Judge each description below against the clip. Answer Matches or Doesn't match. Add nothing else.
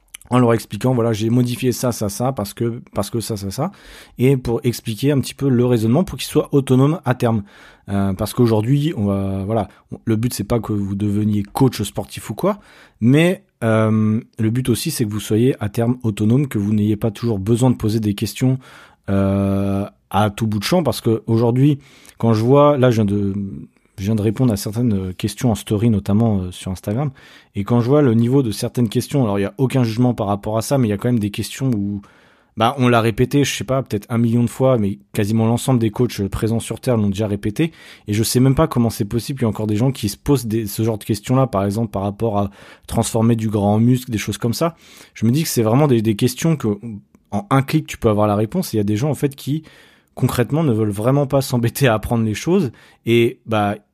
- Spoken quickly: Matches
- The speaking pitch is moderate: Doesn't match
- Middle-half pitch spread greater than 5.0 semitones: Doesn't match